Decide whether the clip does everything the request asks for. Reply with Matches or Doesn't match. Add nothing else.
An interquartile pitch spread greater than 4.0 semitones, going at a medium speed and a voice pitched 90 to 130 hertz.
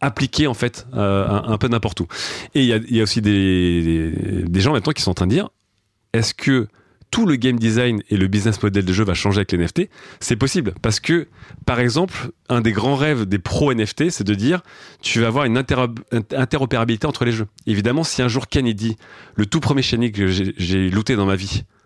Doesn't match